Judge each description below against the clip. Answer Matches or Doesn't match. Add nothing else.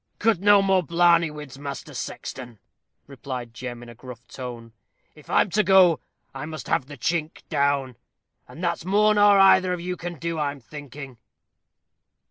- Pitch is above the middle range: Doesn't match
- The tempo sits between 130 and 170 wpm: Matches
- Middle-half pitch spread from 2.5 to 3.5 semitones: Doesn't match